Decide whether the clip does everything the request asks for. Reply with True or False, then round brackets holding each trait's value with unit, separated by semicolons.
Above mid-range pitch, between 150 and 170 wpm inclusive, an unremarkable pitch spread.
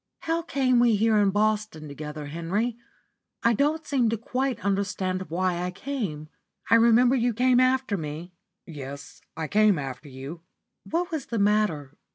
False (210 Hz; 160 wpm; 7.1 semitones)